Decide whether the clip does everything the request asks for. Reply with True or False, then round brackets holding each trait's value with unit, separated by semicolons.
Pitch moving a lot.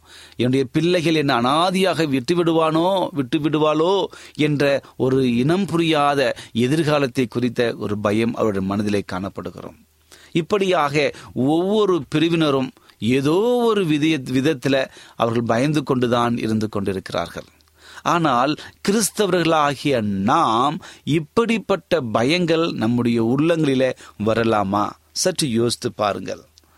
True (6.0 semitones)